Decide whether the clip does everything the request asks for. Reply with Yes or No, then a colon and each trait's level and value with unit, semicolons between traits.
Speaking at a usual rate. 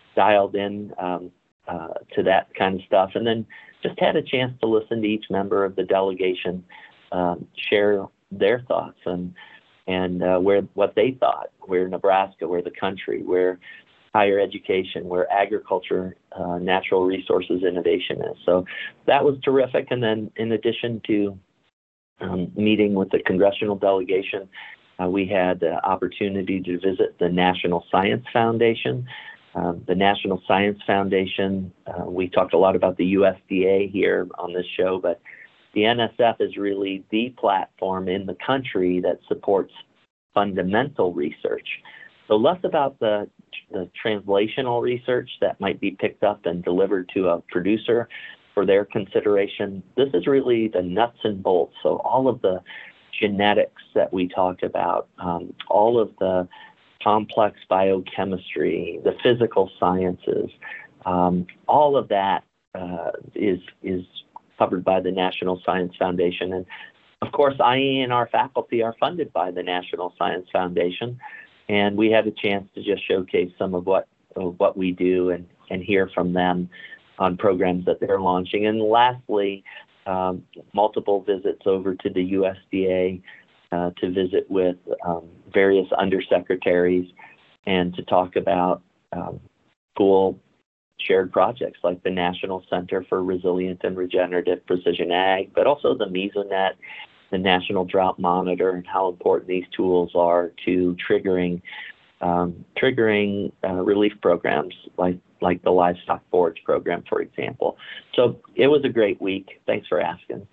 Yes: average, 150 wpm